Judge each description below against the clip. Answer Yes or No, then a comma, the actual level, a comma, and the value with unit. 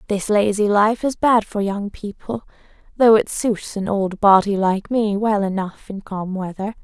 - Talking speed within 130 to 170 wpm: No, average, 185 wpm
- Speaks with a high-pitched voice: Yes, high, 205 Hz